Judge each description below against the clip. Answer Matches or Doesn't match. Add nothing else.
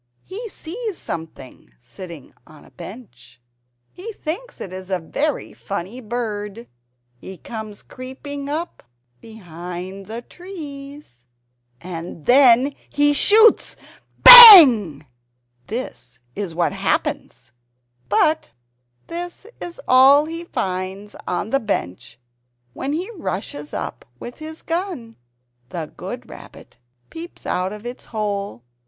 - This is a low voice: Doesn't match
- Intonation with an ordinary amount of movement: Doesn't match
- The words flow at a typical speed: Doesn't match